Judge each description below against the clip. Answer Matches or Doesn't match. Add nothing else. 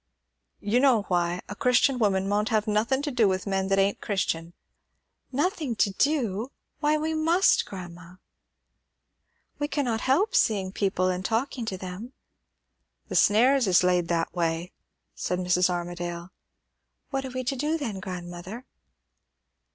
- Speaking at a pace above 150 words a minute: Doesn't match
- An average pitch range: Doesn't match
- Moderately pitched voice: Doesn't match